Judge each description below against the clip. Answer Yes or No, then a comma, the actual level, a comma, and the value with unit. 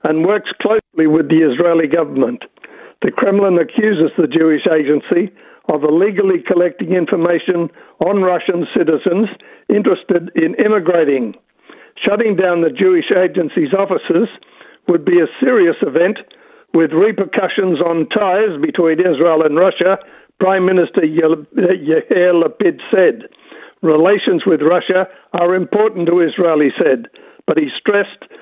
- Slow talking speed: Yes, slow, 125 wpm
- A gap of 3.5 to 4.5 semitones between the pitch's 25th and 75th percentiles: Yes, average, 4.2 semitones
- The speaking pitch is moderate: Yes, medium, 180 Hz